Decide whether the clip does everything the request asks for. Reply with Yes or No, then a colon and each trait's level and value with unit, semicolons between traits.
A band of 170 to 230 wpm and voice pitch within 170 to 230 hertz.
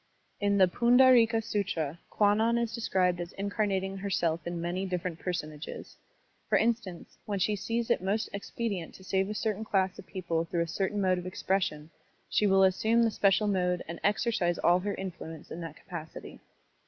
Yes: average, 180 wpm; high, 190 Hz